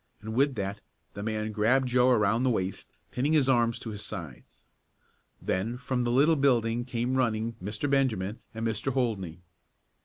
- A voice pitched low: Yes, low, 115 Hz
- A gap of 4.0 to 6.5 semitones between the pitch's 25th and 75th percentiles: No, average, 3.3 semitones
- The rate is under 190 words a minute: Yes, average, 165 wpm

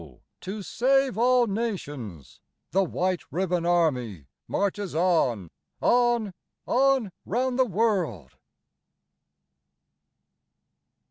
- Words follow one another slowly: Yes, slow, 80 wpm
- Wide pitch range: Yes, wide, 6.6 semitones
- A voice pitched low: No, high, 195 Hz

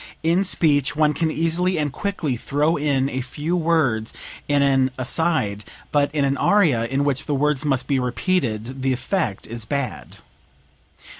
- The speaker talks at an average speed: Yes, average, 160 wpm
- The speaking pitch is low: No, medium, 145 Hz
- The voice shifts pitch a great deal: No, average, 3.6 semitones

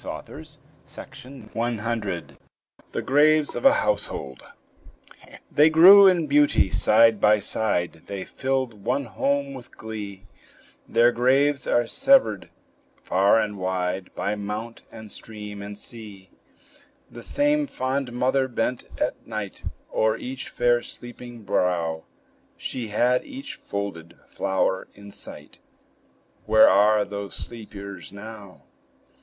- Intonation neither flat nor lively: Yes, average, 4.6 semitones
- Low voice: Yes, low, 110 Hz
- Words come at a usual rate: No, slow, 115 wpm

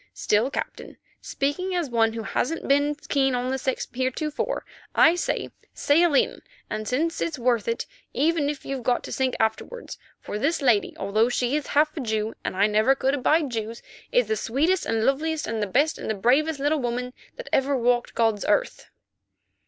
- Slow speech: No, average, 185 wpm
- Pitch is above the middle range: Yes, very high, 265 Hz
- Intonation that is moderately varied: Yes, average, 4.7 semitones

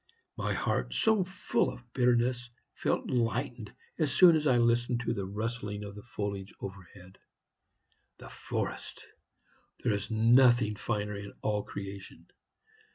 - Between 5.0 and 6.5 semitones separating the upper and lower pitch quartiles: No, average, 3.4 semitones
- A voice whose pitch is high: No, low, 115 Hz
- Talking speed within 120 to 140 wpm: Yes, slow, 135 wpm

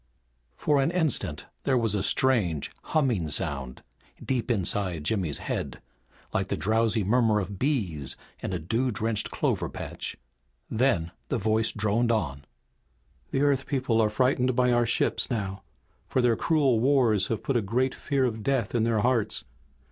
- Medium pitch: No, low, 115 Hz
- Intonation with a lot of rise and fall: No, average, 4.4 semitones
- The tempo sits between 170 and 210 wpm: No, average, 160 wpm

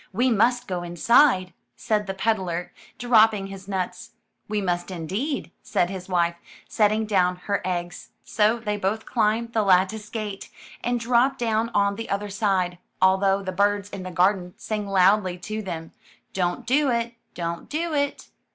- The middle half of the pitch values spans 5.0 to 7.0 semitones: No, average, 3.4 semitones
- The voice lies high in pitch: Yes, high, 200 Hz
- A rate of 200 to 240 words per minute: No, average, 165 wpm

